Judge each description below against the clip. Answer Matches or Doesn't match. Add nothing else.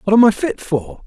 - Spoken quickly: Matches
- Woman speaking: Doesn't match